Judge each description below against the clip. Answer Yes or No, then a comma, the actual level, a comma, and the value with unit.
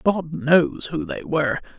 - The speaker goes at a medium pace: Yes, average, 170 wpm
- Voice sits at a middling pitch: Yes, medium, 170 Hz